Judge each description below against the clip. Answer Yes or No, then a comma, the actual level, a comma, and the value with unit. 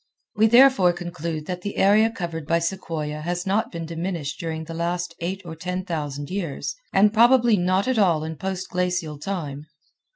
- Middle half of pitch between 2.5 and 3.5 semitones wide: Yes, average, 3.2 semitones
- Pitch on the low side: No, medium, 175 Hz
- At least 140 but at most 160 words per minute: No, average, 175 wpm